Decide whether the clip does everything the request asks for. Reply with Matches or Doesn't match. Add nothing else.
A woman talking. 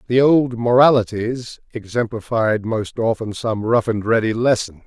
Doesn't match